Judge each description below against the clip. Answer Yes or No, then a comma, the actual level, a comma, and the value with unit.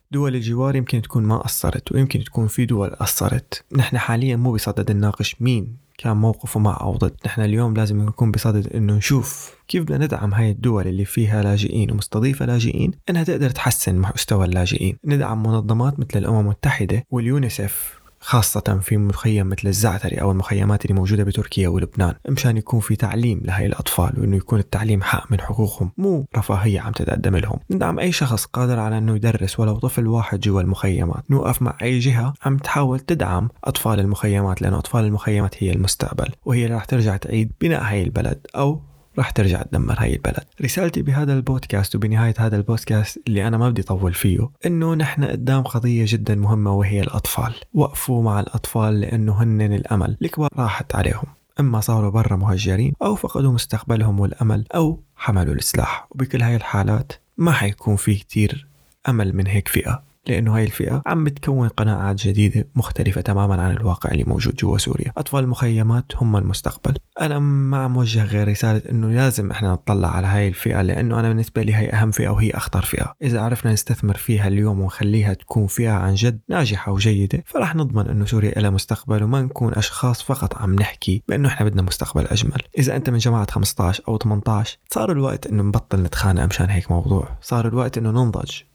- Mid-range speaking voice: No, low, 110 Hz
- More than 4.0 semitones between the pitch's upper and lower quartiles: No, average, 3.7 semitones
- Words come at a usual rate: No, fast, 175 wpm